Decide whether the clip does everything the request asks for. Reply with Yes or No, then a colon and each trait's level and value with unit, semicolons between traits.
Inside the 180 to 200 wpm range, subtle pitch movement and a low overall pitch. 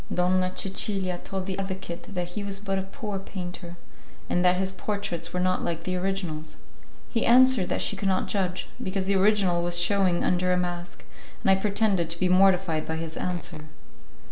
No: average, 190 wpm; narrow, 1.8 semitones; medium, 185 Hz